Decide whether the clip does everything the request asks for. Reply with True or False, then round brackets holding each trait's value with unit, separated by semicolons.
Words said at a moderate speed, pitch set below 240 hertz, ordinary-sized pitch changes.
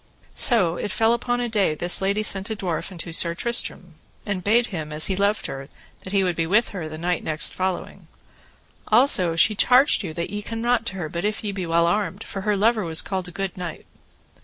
False (230 wpm; 190 Hz; 4.0 semitones)